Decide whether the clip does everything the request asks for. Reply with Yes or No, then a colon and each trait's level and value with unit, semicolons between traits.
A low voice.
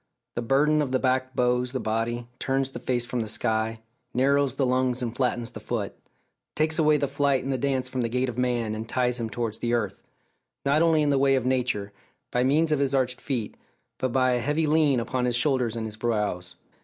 Yes: low, 125 Hz